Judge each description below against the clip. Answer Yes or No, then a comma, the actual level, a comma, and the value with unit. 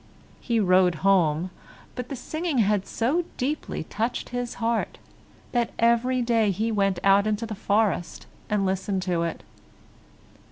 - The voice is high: Yes, high, 215 Hz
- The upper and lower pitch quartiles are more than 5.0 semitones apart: No, average, 3.7 semitones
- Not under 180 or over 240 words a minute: No, average, 145 wpm